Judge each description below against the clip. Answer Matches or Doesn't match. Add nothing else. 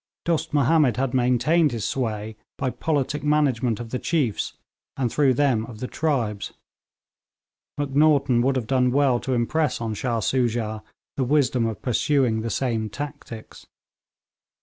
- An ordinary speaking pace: Matches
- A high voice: Doesn't match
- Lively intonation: Doesn't match